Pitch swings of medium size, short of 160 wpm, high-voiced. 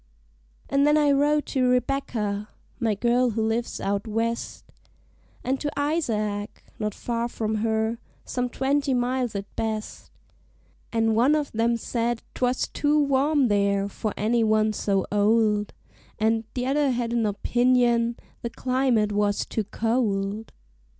Yes: average, 3.1 semitones; average, 140 wpm; high, 230 Hz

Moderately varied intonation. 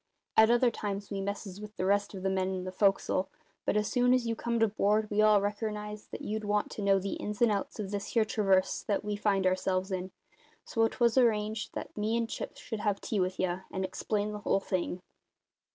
No: narrow, 1.9 semitones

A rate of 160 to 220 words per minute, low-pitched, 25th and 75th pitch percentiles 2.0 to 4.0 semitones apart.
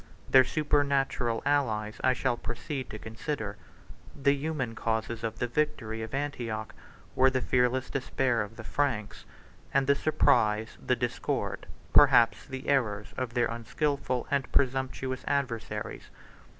No: slow, 135 wpm; low, 125 Hz; average, 3.6 semitones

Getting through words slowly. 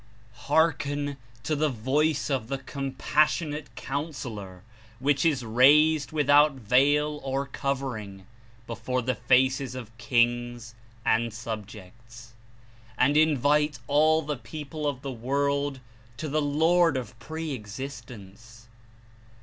Yes: slow, 115 wpm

